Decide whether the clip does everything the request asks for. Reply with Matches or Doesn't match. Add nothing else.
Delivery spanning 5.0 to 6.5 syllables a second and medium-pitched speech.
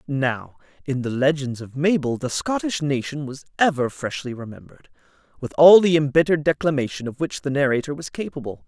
Matches